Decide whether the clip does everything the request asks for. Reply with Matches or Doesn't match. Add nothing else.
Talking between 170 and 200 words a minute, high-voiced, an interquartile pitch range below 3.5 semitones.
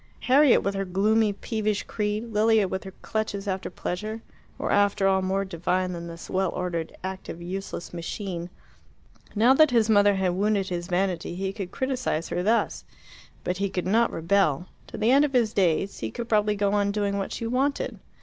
Matches